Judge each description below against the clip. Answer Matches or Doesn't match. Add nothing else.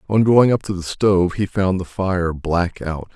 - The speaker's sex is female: Doesn't match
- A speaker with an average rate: Doesn't match